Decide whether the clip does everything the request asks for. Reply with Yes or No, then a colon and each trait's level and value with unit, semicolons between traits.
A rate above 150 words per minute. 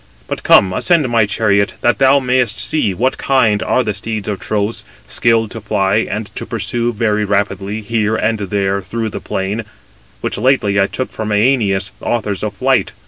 Yes: average, 180 wpm